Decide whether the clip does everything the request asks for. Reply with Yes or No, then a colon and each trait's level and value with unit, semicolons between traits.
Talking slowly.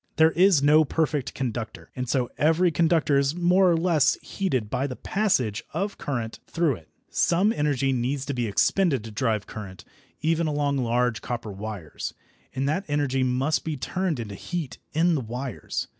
No: average, 175 wpm